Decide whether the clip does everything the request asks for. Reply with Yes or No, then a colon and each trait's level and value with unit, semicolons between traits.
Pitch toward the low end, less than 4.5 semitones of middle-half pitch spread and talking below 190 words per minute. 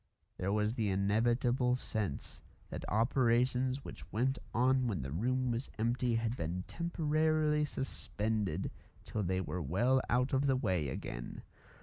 No: low, 120 Hz; average, 4.8 semitones; average, 140 wpm